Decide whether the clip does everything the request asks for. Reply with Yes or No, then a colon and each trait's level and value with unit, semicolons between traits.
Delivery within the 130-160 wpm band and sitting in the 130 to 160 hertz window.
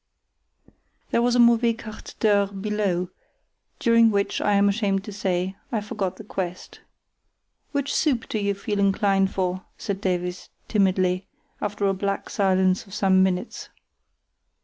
No: average, 145 wpm; high, 200 Hz